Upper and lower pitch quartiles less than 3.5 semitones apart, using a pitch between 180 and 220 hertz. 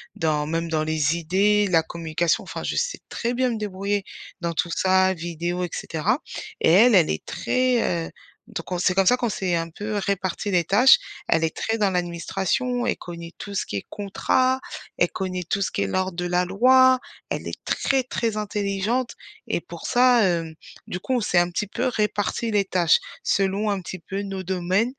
No: average, 3.8 semitones; high, 190 Hz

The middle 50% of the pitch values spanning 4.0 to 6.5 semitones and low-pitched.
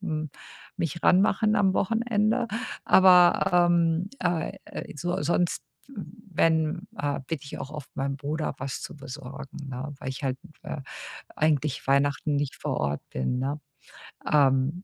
No: average, 4.5 semitones; medium, 155 Hz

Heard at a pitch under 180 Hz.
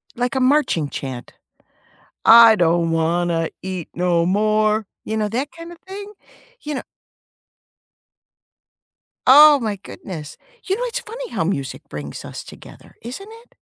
No: high, 215 Hz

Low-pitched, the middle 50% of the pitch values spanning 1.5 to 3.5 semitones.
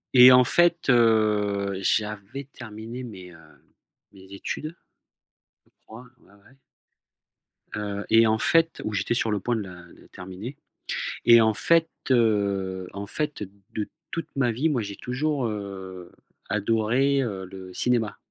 No: low, 110 Hz; average, 4.0 semitones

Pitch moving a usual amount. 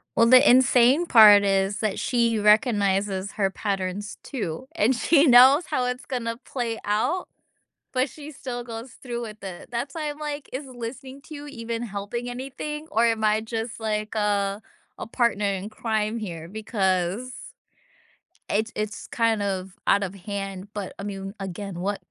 Yes: average, 3.7 semitones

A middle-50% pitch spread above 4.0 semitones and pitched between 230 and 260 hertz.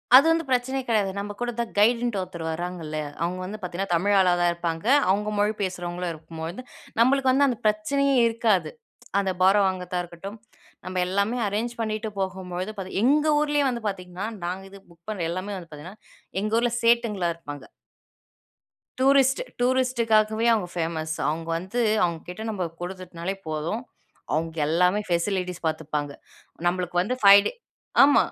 No: average, 4.5 semitones; high, 190 Hz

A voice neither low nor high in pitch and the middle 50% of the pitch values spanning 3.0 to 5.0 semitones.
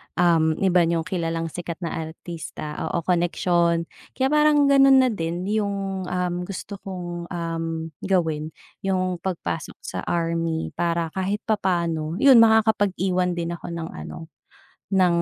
No: medium, 175 Hz; narrow, 2.6 semitones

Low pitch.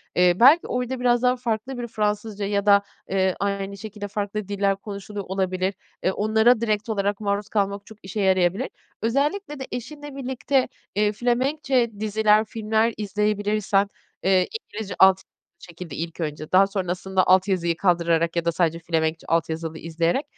No: high, 205 Hz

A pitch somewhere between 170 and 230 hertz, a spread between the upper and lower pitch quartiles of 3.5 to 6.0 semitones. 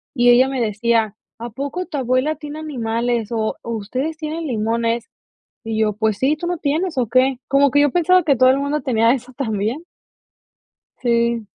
No: very high, 255 Hz; average, 4.1 semitones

